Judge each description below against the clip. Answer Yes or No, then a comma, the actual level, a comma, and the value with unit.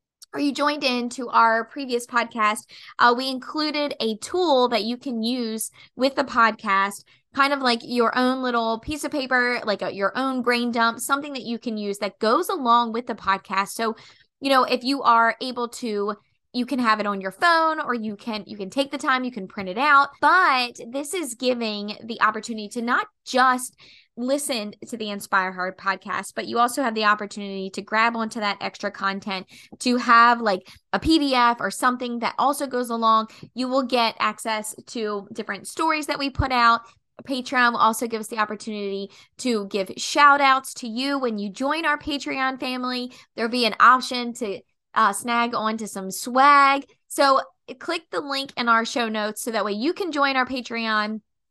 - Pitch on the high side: Yes, high, 240 Hz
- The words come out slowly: No, average, 195 wpm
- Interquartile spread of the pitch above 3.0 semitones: Yes, average, 3.7 semitones